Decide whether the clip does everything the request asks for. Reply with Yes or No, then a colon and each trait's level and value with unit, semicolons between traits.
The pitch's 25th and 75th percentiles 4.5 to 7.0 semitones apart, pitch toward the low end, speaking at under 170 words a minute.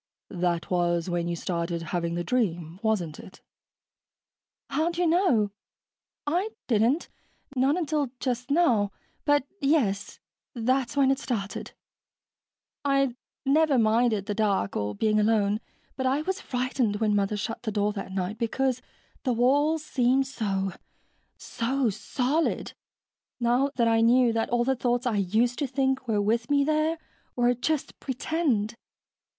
No: average, 4.9 semitones; high, 240 Hz; average, 140 wpm